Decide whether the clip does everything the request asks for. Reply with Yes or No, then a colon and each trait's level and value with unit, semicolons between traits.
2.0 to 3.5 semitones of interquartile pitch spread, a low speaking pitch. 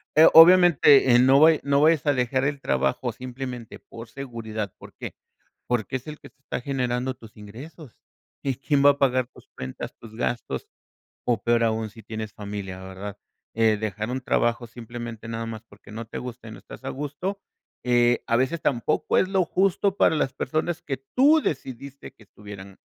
No: average, 4.2 semitones; low, 125 Hz